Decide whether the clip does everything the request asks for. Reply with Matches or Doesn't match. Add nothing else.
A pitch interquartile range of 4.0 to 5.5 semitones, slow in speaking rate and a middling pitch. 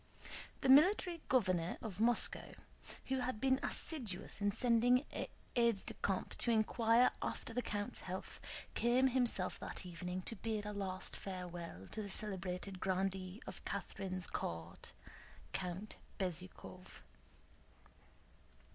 Doesn't match